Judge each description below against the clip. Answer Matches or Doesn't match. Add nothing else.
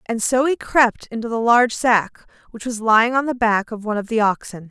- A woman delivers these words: Matches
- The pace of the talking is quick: Matches